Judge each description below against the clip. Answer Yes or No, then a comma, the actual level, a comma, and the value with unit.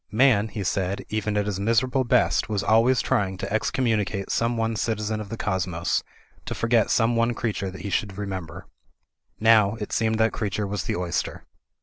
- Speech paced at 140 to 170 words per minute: No, average, 185 wpm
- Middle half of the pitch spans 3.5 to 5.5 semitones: No, narrow, 2.6 semitones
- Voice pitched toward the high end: No, low, 105 Hz